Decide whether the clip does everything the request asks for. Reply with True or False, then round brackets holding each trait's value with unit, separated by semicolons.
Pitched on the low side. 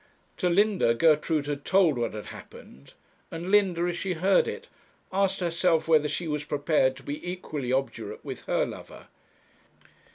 False (165 Hz)